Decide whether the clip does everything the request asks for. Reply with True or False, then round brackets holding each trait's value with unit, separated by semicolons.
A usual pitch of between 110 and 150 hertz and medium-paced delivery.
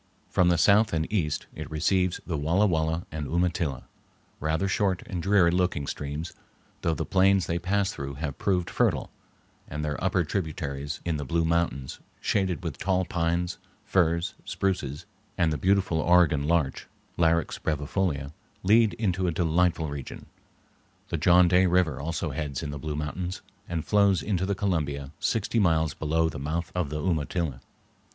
False (85 Hz; 160 wpm)